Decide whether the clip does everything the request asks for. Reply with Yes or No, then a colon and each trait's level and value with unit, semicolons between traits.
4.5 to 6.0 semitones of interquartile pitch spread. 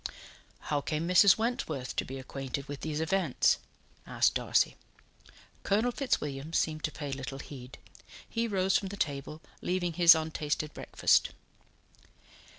Yes: average, 4.9 semitones